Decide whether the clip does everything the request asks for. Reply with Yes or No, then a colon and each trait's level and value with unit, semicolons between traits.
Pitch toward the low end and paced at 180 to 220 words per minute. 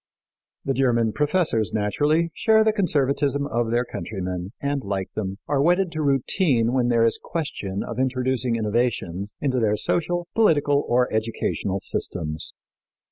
No: low, 125 Hz; average, 140 wpm